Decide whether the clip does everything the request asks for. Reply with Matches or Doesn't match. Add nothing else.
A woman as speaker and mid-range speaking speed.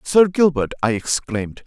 Doesn't match